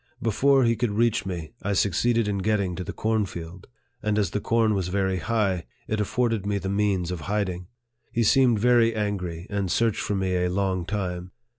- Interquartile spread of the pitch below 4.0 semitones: Yes, average, 3.2 semitones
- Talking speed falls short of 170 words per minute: No, average, 190 wpm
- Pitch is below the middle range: Yes, low, 100 Hz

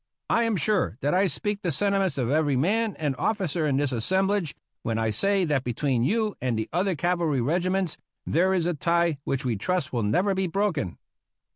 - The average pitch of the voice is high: No, medium, 170 Hz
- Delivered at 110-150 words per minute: No, average, 200 wpm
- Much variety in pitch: Yes, wide, 6.1 semitones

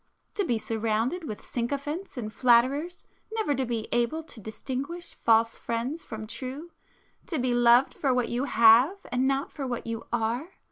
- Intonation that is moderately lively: Yes, average, 3.9 semitones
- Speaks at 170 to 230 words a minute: No, average, 155 wpm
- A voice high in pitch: Yes, very high, 250 Hz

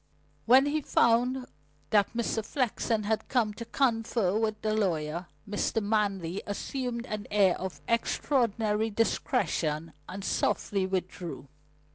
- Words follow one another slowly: Yes, slow, 120 wpm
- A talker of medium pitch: No, high, 215 Hz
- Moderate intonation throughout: Yes, average, 3.5 semitones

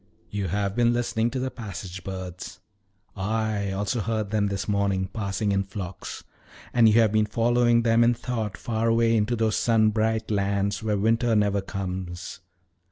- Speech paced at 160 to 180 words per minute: Yes, average, 165 wpm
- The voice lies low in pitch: Yes, low, 105 Hz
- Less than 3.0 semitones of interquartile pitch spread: Yes, narrow, 2.5 semitones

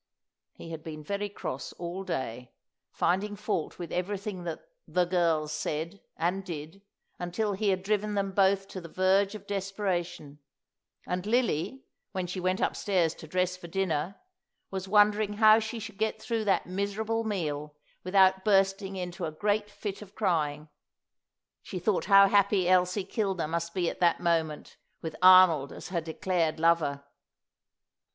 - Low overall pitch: No, medium, 185 Hz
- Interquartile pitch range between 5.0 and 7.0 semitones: No, average, 3.2 semitones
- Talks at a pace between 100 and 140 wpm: No, average, 155 wpm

